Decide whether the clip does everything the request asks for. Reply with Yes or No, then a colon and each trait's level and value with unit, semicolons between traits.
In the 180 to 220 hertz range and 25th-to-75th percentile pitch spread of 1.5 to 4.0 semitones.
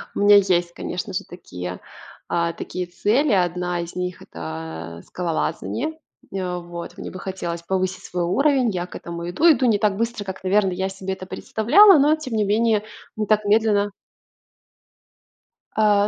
Yes: high, 190 Hz; average, 3.7 semitones